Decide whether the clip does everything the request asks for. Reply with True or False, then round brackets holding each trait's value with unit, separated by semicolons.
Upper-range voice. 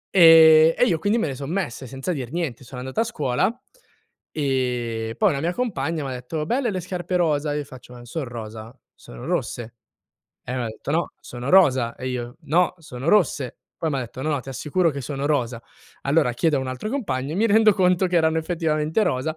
False (145 Hz)